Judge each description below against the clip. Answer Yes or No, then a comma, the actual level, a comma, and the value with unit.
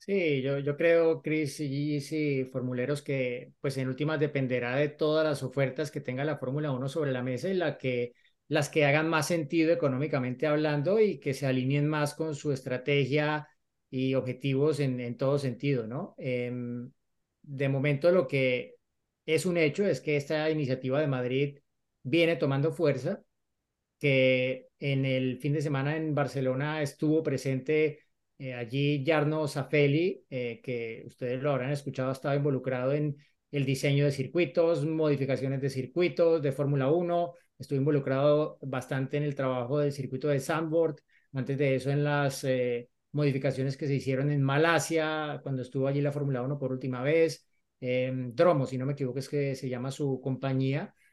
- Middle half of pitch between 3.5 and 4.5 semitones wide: No, narrow, 2.6 semitones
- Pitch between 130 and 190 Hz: Yes, medium, 140 Hz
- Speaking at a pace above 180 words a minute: No, average, 175 wpm